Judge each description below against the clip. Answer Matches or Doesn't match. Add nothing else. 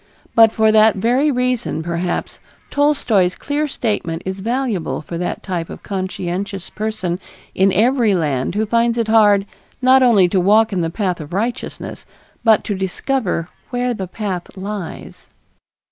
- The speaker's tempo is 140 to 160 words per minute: Matches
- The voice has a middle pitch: Doesn't match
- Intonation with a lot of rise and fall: Doesn't match